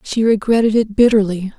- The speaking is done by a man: No, female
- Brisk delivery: No, average, 150 wpm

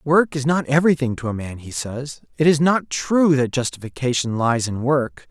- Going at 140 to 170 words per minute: No, fast, 205 wpm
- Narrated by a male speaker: Yes, male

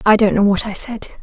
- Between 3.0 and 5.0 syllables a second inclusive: No, 5.9 syllables/s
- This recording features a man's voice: No, female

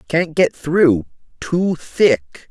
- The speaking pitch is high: No, medium, 150 Hz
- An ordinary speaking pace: No, slow, 95 wpm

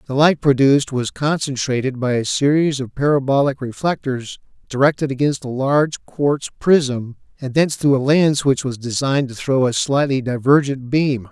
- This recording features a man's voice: Yes, male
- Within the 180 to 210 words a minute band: No, average, 165 wpm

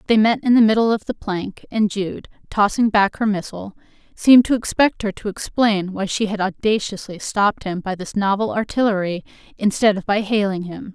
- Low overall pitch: No, high, 205 Hz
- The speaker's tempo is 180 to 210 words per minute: Yes, average, 190 wpm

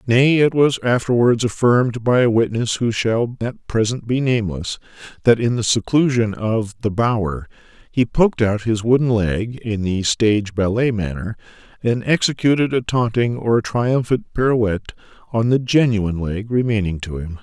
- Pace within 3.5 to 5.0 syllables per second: Yes, 4.8 syllables/s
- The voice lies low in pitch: Yes, low, 115 Hz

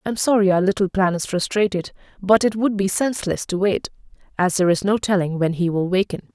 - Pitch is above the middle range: Yes, high, 195 Hz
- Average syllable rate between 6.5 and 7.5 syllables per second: No, 6.0 syllables/s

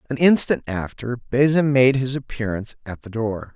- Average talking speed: Yes, average, 170 wpm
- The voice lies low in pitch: Yes, low, 125 Hz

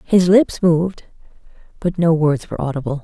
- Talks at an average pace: Yes, average, 160 wpm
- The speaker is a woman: Yes, female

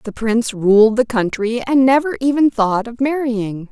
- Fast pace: No, average, 180 wpm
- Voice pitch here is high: Yes, high, 235 Hz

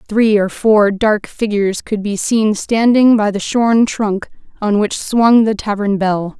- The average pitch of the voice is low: No, high, 210 Hz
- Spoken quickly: No, average, 180 wpm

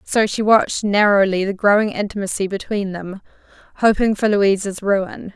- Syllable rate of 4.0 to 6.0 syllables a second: Yes, 4.9 syllables/s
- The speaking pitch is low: No, high, 200 Hz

